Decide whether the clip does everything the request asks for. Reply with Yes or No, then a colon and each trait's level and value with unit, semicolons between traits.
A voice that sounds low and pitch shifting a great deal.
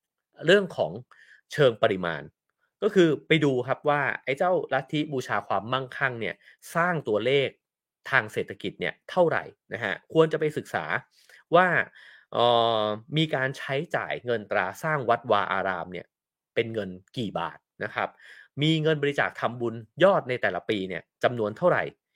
Yes: low, 130 Hz; wide, 6.3 semitones